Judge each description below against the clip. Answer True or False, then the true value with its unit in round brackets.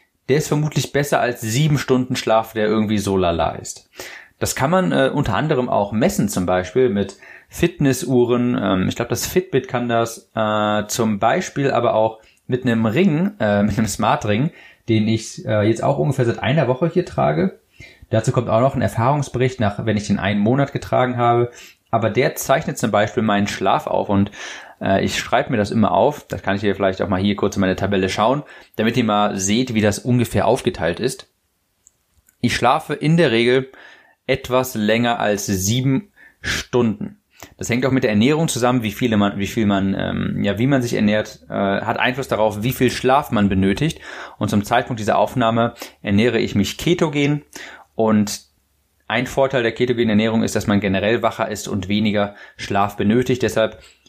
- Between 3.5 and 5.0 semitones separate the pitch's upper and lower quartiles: True (3.8 semitones)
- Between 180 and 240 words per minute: True (190 wpm)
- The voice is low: True (115 Hz)